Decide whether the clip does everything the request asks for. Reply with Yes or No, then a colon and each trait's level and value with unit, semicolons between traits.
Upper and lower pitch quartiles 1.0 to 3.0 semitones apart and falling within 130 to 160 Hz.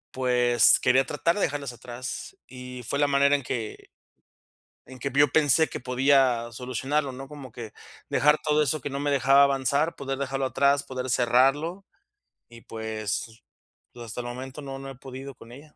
Yes: narrow, 2.4 semitones; low, 135 Hz